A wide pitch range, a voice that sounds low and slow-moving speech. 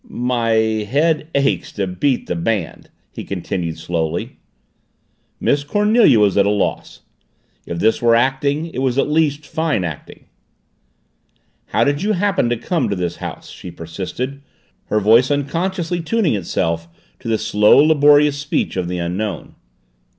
No: wide, 7.0 semitones; low, 120 Hz; average, 150 wpm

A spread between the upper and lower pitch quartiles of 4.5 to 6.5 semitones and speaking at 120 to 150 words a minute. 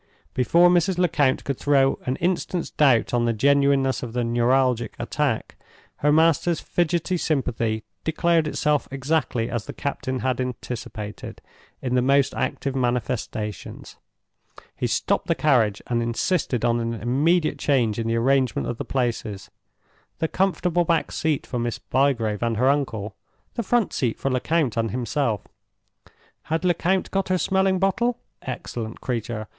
Yes: average, 5.3 semitones; average, 145 wpm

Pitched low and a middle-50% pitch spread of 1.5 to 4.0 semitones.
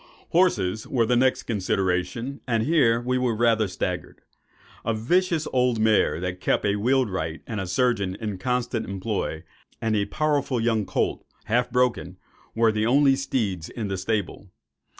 No: low, 115 Hz; average, 4.4 semitones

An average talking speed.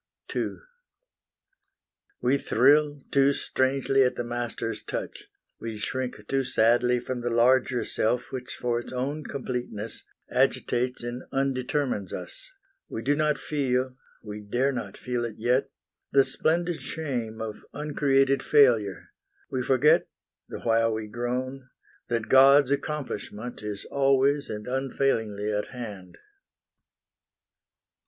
No: slow, 120 wpm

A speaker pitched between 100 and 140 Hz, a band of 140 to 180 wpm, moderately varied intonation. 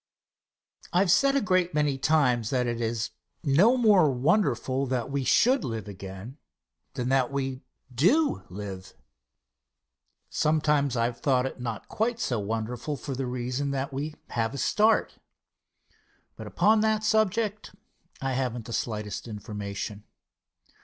No: low, 135 Hz; average, 145 wpm; wide, 6.7 semitones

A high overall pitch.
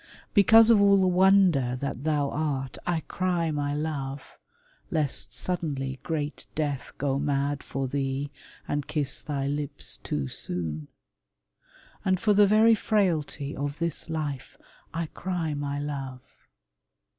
No: medium, 145 Hz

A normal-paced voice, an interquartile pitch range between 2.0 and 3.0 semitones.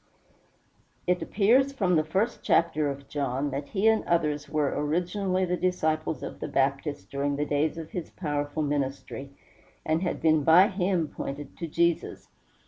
No: average, 165 wpm; average, 3.7 semitones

